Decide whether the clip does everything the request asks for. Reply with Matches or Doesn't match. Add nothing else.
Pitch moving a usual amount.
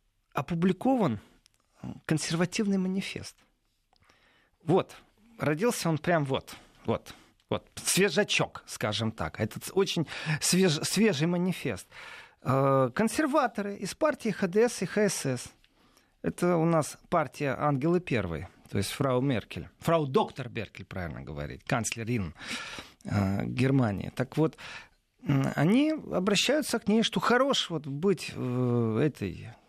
Doesn't match